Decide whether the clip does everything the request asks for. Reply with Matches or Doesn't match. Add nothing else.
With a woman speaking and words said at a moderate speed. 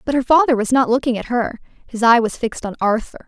Doesn't match